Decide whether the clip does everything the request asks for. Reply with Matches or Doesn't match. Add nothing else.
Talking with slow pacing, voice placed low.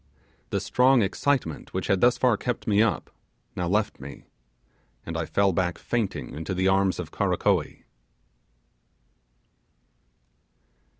Matches